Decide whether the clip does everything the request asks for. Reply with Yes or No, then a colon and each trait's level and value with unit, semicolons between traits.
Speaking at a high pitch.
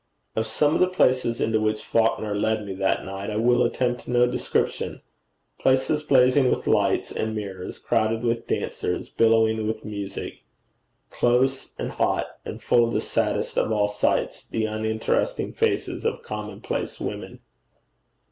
No: low, 115 Hz